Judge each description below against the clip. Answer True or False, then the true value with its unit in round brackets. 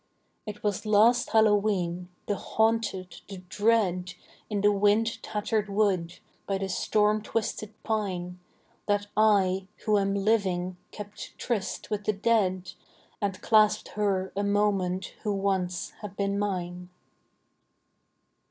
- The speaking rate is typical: False (125 wpm)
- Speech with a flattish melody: True (2.3 semitones)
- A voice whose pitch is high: True (200 Hz)